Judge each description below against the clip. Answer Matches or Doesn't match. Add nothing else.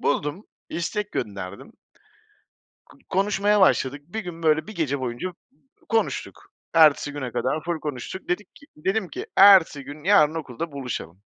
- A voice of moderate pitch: Matches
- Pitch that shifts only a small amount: Doesn't match